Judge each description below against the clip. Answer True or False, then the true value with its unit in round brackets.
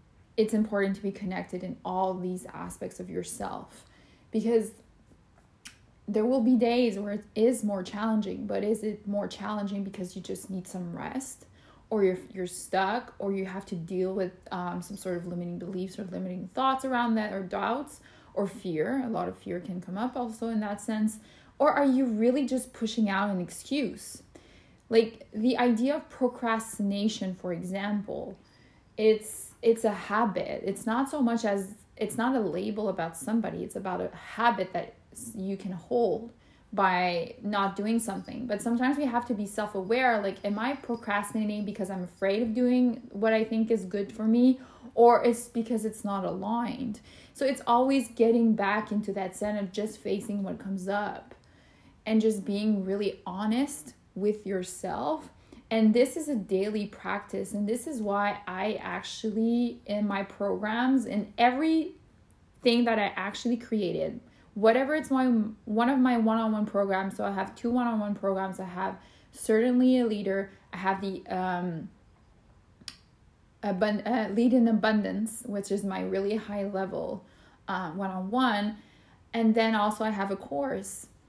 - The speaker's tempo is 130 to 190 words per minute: True (165 wpm)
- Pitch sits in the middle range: False (215 Hz)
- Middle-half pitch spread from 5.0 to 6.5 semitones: False (3.2 semitones)